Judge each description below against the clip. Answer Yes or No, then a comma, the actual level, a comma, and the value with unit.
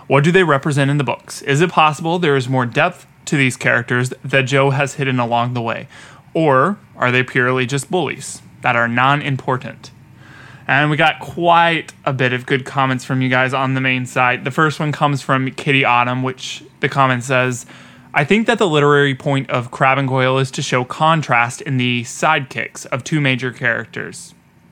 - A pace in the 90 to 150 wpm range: No, average, 200 wpm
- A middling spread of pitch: No, narrow, 2.3 semitones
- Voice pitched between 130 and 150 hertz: Yes, low, 135 Hz